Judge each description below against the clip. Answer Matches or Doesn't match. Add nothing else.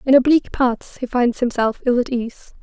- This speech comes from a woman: Matches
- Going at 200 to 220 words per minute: Matches